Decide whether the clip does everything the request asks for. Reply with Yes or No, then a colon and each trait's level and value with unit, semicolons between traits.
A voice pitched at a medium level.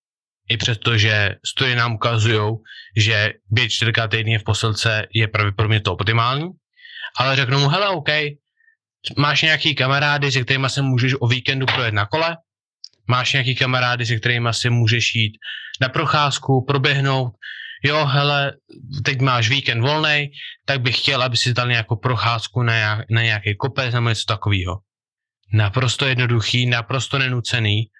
No: low, 125 Hz